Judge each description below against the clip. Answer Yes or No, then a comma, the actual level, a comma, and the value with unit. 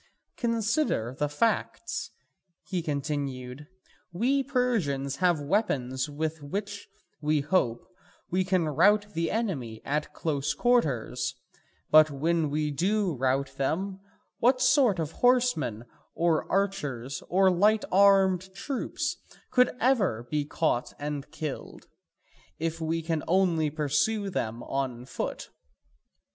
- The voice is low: No, medium, 160 Hz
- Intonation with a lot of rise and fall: Yes, wide, 6.0 semitones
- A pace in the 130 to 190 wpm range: No, slow, 115 wpm